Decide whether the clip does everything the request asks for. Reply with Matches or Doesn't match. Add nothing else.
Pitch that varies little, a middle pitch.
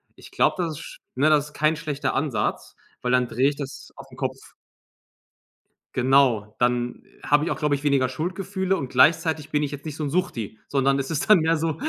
Doesn't match